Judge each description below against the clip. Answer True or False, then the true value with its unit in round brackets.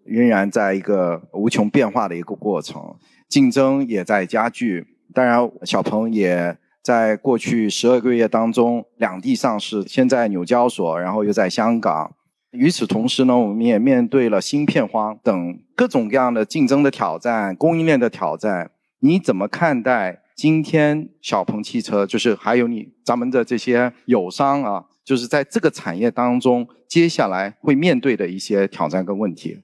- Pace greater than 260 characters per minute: False (255 characters per minute)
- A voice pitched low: True (120 Hz)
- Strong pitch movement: False (4.3 semitones)